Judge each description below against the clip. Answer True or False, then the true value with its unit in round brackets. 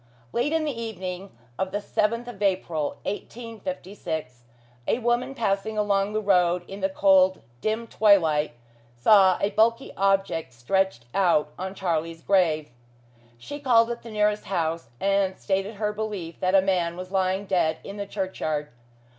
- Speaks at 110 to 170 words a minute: True (155 wpm)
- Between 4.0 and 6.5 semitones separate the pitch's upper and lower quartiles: False (3.1 semitones)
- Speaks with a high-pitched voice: True (195 Hz)